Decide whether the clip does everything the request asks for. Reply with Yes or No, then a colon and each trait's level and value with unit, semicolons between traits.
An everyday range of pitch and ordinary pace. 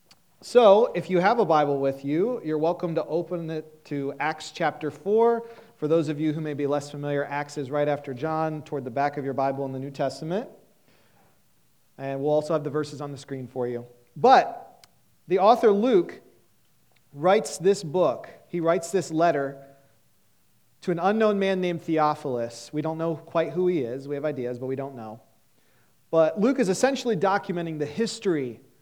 Yes: average, 3.9 semitones; average, 185 wpm